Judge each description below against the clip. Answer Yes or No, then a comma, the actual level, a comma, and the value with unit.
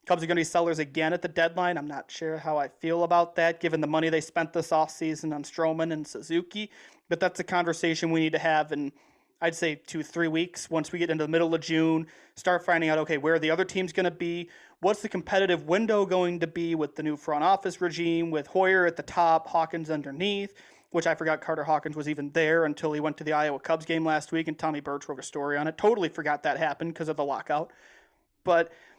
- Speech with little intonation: Yes, narrow, 1.8 semitones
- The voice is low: No, medium, 165 Hz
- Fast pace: Yes, fast, 245 wpm